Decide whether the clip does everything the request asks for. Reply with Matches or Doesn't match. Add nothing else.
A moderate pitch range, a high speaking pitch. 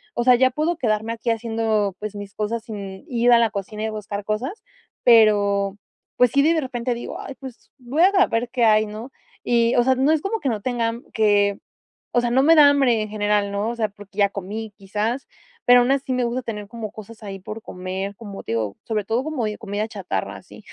Matches